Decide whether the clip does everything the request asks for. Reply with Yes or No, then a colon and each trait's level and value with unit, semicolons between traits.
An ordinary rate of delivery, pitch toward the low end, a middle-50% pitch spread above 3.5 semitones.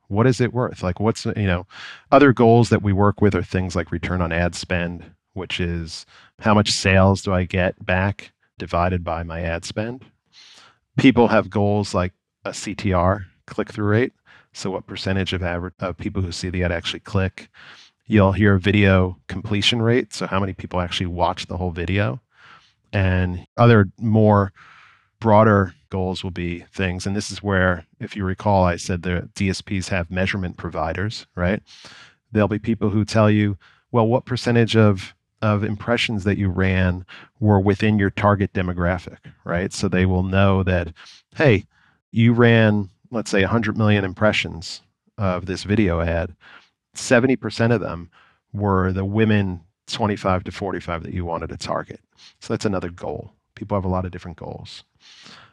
No: average, 170 wpm; low, 100 Hz; average, 2.9 semitones